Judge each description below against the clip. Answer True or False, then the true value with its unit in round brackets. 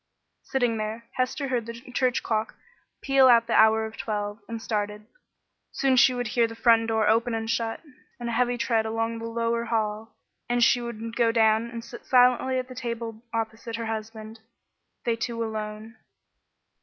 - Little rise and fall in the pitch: True (1.4 semitones)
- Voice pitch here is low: False (230 Hz)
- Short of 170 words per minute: False (180 wpm)